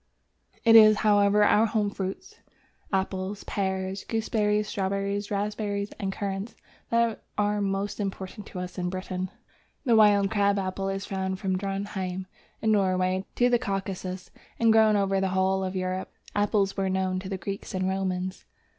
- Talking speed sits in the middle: Yes, average, 155 wpm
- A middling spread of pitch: No, narrow, 1.6 semitones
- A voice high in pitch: Yes, high, 195 Hz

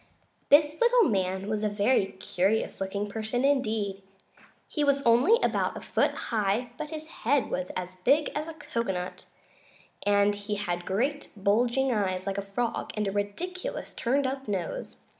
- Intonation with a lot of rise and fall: Yes, wide, 5.8 semitones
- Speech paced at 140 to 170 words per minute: Yes, average, 160 wpm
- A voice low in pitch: No, high, 215 Hz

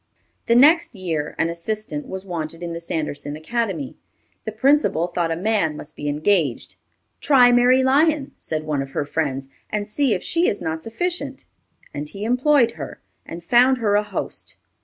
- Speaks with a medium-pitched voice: No, high, 195 Hz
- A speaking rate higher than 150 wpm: Yes, average, 175 wpm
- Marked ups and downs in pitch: Yes, wide, 7.4 semitones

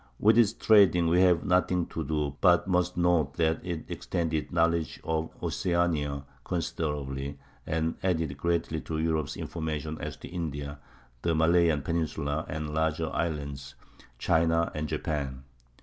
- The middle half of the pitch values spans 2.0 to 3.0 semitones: Yes, narrow, 2.4 semitones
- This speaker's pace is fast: No, slow, 135 wpm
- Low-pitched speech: Yes, very low, 80 Hz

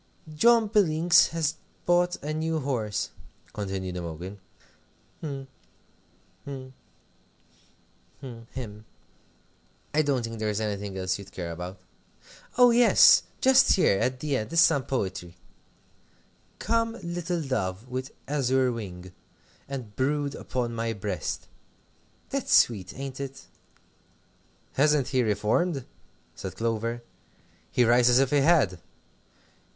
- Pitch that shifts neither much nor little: No, wide, 6.5 semitones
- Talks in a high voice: No, low, 130 Hz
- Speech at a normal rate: No, slow, 120 wpm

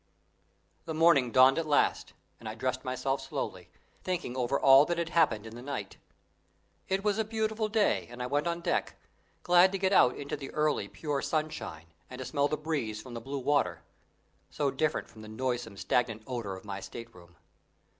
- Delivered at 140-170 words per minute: No, average, 195 wpm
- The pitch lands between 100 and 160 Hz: Yes, medium, 140 Hz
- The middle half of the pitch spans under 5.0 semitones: No, wide, 5.6 semitones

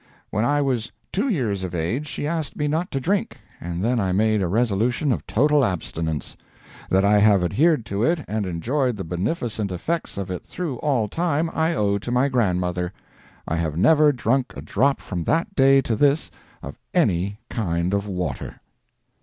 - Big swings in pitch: Yes, wide, 7.5 semitones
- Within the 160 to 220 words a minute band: Yes, average, 185 wpm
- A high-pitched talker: No, low, 115 Hz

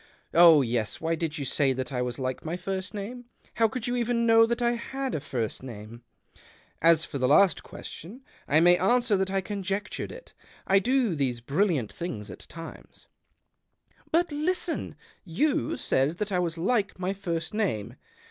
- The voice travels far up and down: Yes, wide, 7.9 semitones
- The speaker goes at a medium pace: Yes, average, 185 wpm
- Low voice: No, medium, 180 Hz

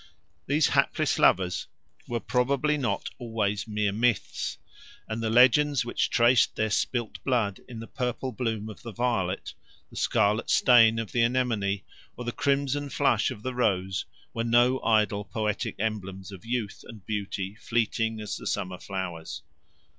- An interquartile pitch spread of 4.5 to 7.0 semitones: No, average, 3.3 semitones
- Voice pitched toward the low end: Yes, low, 115 Hz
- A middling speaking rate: Yes, average, 155 wpm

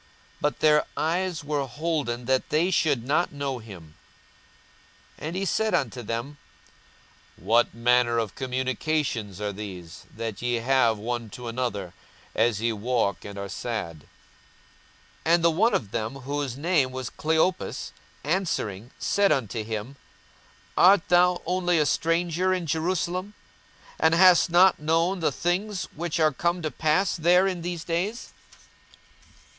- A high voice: No, medium, 145 Hz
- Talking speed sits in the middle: Yes, average, 145 wpm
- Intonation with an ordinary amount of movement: No, wide, 6.8 semitones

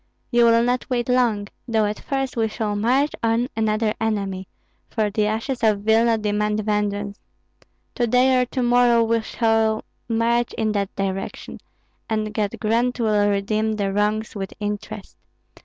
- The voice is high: Yes, high, 220 Hz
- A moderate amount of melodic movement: No, narrow, 2.2 semitones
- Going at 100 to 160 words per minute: Yes, average, 155 wpm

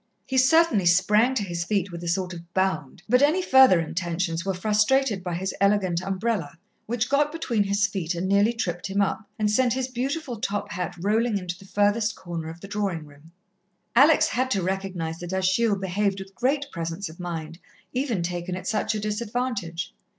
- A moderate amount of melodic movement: Yes, average, 4.7 semitones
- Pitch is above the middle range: Yes, high, 195 Hz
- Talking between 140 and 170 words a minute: No, average, 190 wpm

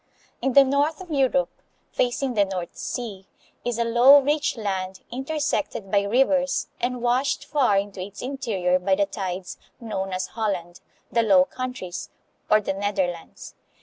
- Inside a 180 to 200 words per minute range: No, average, 150 wpm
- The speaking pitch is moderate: No, high, 225 Hz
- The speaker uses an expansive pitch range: Yes, wide, 5.7 semitones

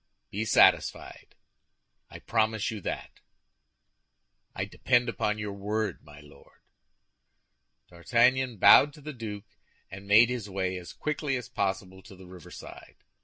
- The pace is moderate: No, slow, 130 wpm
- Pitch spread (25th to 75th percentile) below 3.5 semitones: No, average, 3.9 semitones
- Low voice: Yes, low, 105 Hz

